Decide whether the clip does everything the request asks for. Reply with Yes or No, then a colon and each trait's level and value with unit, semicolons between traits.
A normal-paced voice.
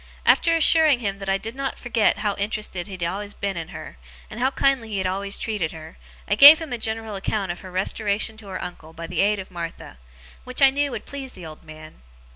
No: fast, 240 wpm